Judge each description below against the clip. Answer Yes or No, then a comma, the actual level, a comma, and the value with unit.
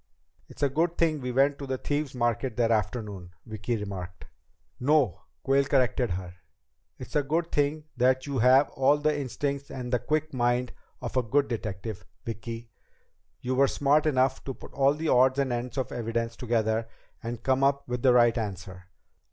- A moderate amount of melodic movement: Yes, average, 3.3 semitones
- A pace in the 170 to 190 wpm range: Yes, average, 180 wpm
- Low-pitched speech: Yes, low, 125 Hz